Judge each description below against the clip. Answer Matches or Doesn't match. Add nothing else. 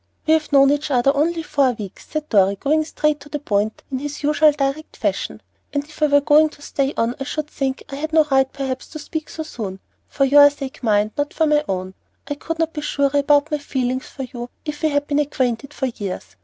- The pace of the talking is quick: Matches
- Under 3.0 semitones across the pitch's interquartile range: Matches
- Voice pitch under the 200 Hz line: Doesn't match